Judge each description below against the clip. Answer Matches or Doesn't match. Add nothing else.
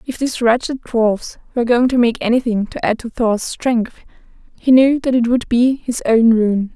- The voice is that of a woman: Matches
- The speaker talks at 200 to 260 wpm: Matches